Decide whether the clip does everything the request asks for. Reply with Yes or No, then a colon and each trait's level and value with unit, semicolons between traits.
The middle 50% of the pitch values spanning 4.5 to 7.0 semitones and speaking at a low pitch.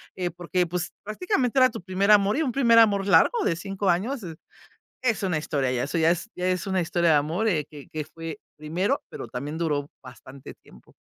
No: average, 4.9 semitones; medium, 175 Hz